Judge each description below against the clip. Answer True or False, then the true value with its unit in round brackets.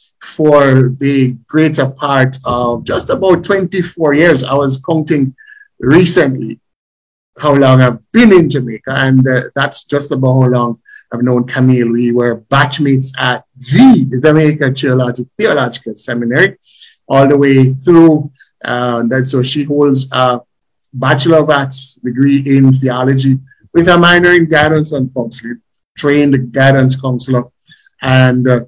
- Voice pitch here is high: False (135 Hz)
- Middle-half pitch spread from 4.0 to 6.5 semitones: False (2.8 semitones)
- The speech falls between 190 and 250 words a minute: False (140 wpm)